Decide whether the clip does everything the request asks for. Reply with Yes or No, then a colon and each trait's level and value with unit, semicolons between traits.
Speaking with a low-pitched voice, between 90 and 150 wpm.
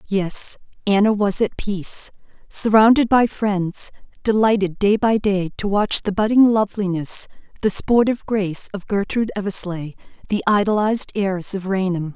No: high, 200 Hz; average, 140 wpm